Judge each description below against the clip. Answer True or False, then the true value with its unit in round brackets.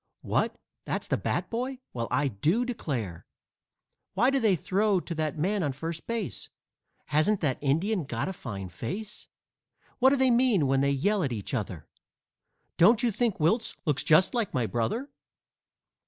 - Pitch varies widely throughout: True (8.5 semitones)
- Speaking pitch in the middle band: True (170 Hz)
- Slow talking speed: False (170 wpm)